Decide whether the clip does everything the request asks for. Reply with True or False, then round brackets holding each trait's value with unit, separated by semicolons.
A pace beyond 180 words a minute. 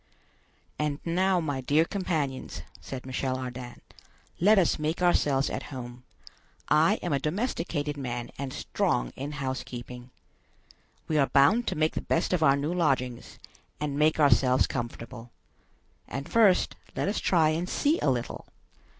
False (150 wpm)